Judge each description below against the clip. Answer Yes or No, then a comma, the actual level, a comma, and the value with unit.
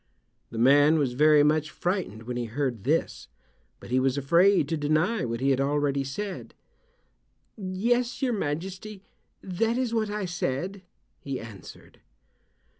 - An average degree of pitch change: No, wide, 6.3 semitones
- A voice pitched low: No, medium, 155 Hz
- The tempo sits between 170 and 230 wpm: No, average, 145 wpm